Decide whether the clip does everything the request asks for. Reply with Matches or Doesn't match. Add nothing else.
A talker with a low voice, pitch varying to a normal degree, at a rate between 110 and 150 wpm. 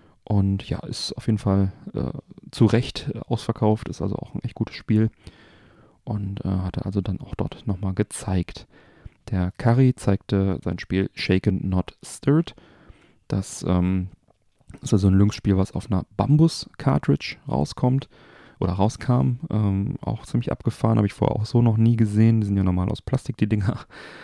Doesn't match